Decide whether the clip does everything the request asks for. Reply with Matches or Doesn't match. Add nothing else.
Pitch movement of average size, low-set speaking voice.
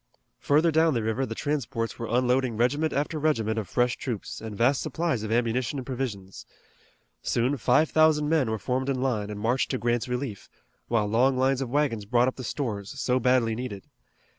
Matches